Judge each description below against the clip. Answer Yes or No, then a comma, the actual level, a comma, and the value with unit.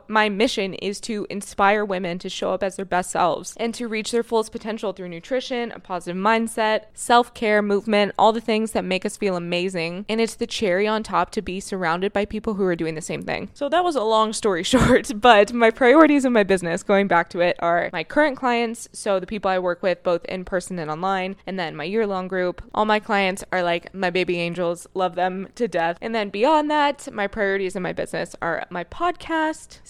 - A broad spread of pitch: No, average, 3.6 semitones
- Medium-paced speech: No, fast, 230 wpm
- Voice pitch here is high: Yes, high, 200 Hz